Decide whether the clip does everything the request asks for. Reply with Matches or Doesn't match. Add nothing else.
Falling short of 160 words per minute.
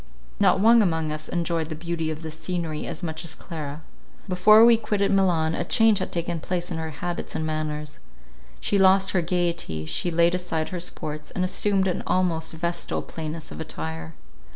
Doesn't match